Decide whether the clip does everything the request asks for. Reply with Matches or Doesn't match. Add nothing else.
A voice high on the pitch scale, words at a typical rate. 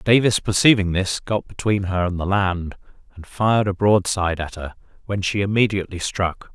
Doesn't match